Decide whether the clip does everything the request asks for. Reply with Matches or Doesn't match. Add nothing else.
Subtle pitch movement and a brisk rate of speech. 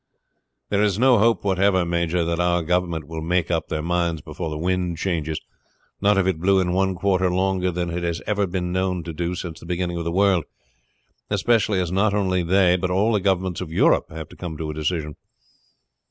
Matches